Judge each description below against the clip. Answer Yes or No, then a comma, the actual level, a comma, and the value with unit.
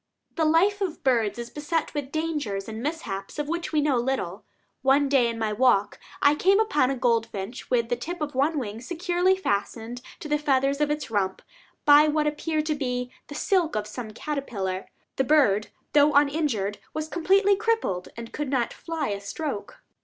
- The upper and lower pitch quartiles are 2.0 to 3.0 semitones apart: No, average, 5.2 semitones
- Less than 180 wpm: No, average, 185 wpm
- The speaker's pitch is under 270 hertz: No, very high, 280 Hz